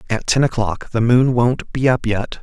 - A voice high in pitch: No, low, 120 Hz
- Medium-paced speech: No, fast, 225 wpm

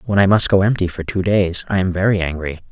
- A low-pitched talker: Yes, very low, 95 Hz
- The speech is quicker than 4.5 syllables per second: Yes, 6.0 syllables/s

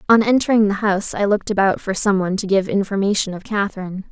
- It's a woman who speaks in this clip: Yes, female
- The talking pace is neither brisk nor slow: No, fast, 220 wpm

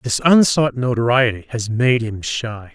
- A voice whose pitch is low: Yes, low, 120 Hz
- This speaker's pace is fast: No, average, 155 wpm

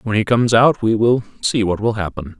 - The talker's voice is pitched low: Yes, low, 110 Hz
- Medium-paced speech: No, fast, 250 wpm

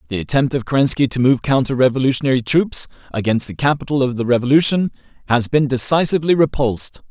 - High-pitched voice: No, low, 130 Hz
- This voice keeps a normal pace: Yes, average, 160 wpm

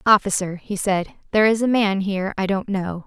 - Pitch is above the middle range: Yes, high, 200 Hz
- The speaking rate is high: Yes, fast, 215 wpm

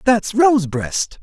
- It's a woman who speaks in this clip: No, male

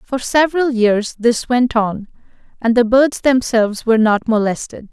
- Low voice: No, high, 235 Hz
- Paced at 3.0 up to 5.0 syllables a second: Yes, 4.7 syllables/s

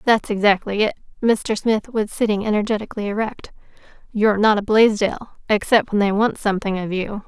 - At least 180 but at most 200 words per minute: No, average, 155 wpm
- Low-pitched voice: No, high, 210 Hz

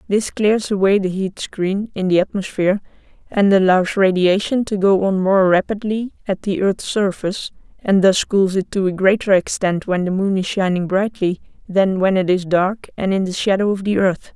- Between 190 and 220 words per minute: Yes, average, 195 wpm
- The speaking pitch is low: No, high, 195 Hz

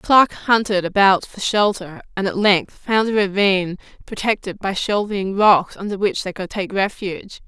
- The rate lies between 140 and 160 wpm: No, average, 170 wpm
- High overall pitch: Yes, high, 195 Hz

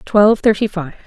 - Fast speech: No, average, 170 wpm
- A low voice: No, high, 200 Hz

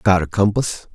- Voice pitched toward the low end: Yes, very low, 95 Hz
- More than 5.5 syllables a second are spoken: No, 4.6 syllables/s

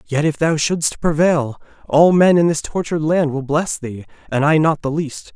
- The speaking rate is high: Yes, fast, 215 wpm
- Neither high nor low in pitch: Yes, medium, 155 Hz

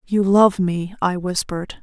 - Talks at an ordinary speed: Yes, average, 165 wpm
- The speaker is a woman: Yes, female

